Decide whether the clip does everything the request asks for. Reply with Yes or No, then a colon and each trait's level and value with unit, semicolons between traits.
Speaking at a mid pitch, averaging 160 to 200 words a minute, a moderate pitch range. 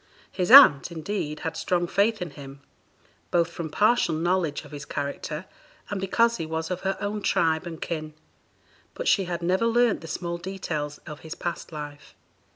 Yes: medium, 170 Hz; average, 175 wpm; average, 3.7 semitones